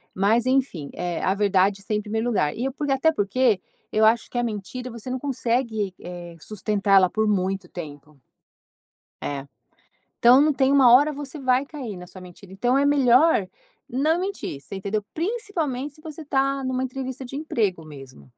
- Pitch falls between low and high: No, high, 235 Hz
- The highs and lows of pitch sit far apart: Yes, wide, 5.8 semitones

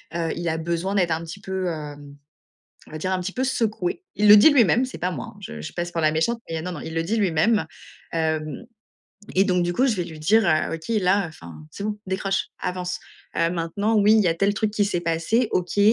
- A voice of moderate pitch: Yes, medium, 180 Hz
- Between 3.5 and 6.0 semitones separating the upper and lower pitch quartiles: Yes, average, 4.0 semitones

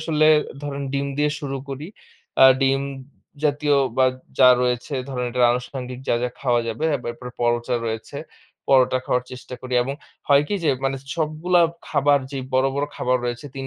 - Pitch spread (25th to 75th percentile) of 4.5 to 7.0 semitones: No, narrow, 2.5 semitones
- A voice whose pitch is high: No, low, 135 Hz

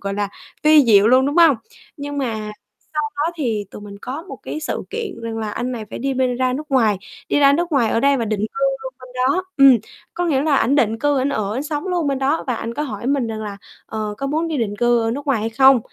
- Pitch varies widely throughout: No, average, 4.3 semitones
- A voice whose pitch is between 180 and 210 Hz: No, very high, 265 Hz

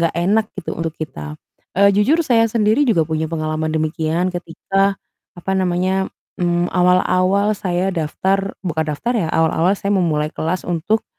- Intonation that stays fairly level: No, average, 3.4 semitones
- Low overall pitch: No, medium, 180 Hz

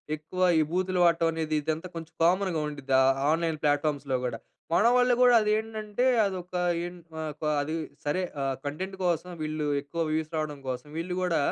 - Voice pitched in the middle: Yes, medium, 165 Hz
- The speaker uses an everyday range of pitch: Yes, average, 3.4 semitones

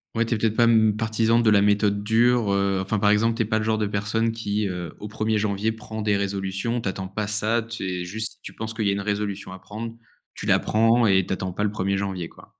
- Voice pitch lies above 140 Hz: No, low, 105 Hz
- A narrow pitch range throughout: Yes, narrow, 2.1 semitones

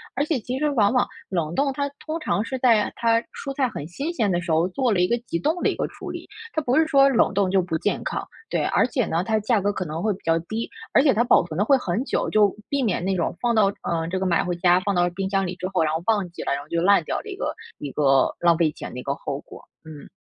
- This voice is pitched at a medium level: No, high, 200 Hz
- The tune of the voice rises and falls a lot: Yes, wide, 6.4 semitones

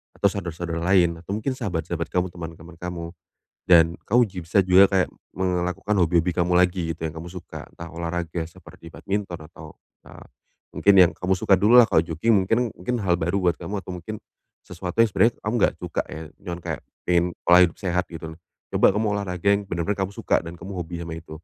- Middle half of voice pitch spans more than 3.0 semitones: No, narrow, 2.5 semitones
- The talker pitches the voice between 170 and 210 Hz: No, very low, 90 Hz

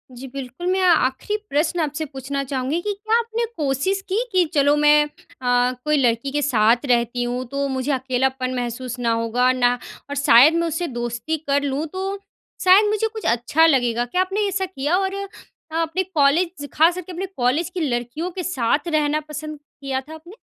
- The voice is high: Yes, very high, 290 Hz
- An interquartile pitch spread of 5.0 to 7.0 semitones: Yes, wide, 5.5 semitones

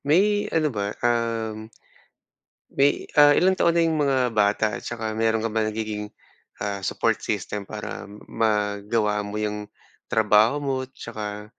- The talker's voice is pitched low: Yes, low, 110 Hz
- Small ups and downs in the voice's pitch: No, average, 3.7 semitones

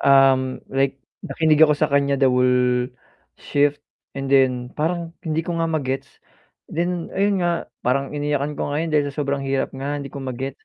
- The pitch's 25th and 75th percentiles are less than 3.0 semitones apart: Yes, narrow, 2.6 semitones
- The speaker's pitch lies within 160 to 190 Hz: No, medium, 140 Hz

